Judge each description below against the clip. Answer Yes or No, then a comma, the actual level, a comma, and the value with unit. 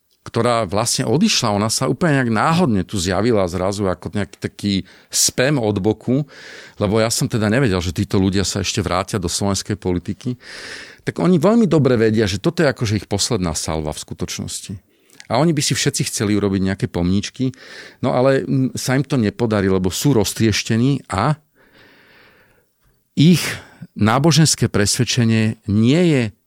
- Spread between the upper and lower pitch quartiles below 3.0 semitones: No, average, 5.0 semitones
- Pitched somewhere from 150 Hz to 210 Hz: No, low, 115 Hz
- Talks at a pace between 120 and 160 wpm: Yes, average, 155 wpm